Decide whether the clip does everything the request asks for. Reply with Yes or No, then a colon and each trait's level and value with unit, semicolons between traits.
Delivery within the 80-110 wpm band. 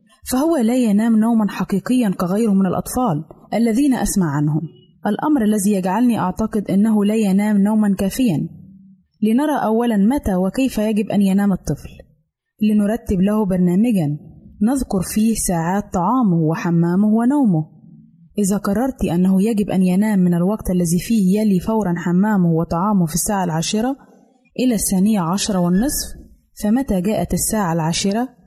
No: average, 130 wpm